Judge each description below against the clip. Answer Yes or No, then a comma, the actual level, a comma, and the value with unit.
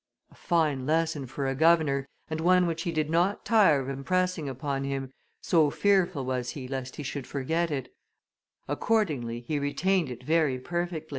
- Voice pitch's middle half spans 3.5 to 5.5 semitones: Yes, average, 4.0 semitones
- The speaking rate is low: No, average, 170 wpm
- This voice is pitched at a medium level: Yes, medium, 150 Hz